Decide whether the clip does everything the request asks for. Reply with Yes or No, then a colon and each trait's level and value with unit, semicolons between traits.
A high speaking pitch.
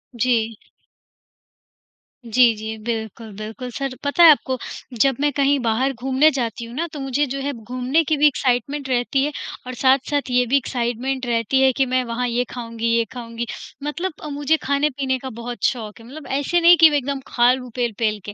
Yes: very high, 255 Hz